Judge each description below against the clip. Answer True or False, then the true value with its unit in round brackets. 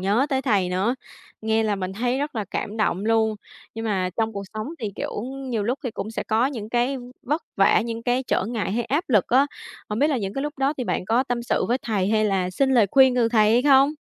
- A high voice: True (230 Hz)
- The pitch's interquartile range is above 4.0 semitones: False (3.7 semitones)